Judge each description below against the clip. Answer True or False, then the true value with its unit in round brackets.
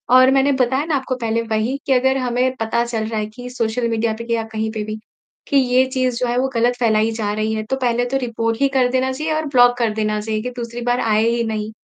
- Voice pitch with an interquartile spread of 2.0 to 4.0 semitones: True (2.6 semitones)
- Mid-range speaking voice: False (240 Hz)